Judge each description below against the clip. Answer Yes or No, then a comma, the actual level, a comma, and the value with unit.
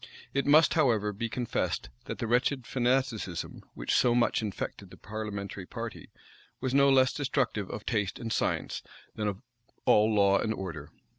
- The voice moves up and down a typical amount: Yes, average, 4.0 semitones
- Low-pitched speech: Yes, low, 110 Hz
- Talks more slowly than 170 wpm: Yes, average, 160 wpm